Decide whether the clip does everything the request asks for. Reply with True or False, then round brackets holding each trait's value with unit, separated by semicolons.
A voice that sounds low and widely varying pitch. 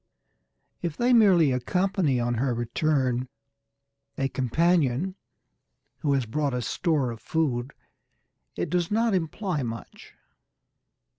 False (145 Hz; 6.1 semitones)